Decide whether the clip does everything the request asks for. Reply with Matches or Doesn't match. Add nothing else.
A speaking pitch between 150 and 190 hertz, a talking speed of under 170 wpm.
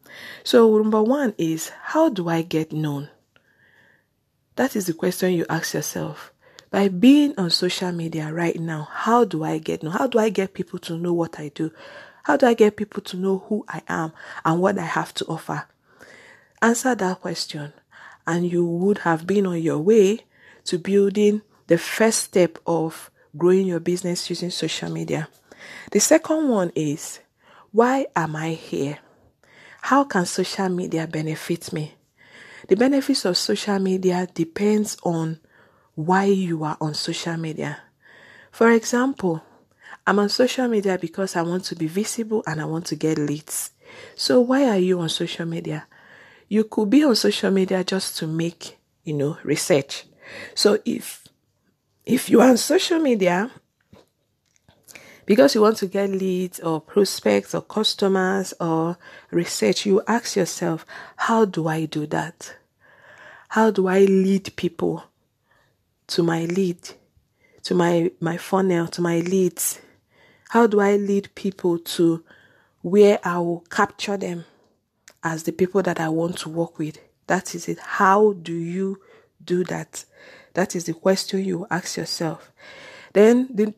Matches